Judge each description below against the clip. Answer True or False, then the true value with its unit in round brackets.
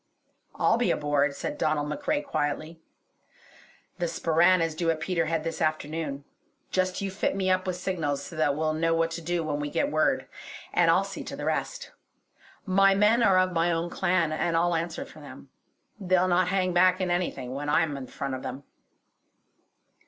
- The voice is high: False (165 Hz)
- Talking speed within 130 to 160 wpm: False (190 wpm)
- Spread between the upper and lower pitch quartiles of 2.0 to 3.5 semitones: True (3.0 semitones)